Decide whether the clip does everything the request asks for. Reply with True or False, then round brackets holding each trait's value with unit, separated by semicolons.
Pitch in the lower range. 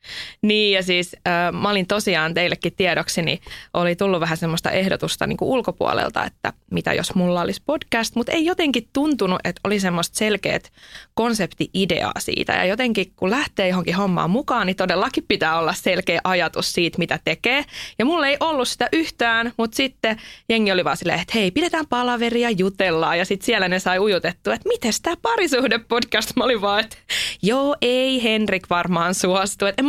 False (205 Hz)